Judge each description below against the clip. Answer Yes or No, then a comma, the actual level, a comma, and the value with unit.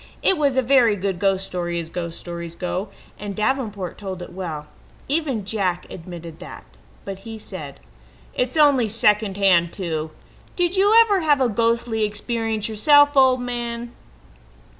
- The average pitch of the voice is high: Yes, high, 215 Hz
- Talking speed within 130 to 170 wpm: Yes, average, 155 wpm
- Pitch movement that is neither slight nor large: No, wide, 5.7 semitones